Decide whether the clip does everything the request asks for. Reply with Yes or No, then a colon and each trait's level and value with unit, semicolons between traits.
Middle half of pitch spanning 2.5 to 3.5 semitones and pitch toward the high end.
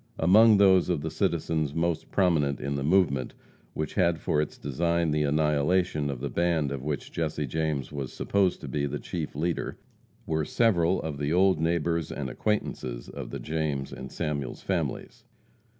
No: average, 3.1 semitones; very low, 80 Hz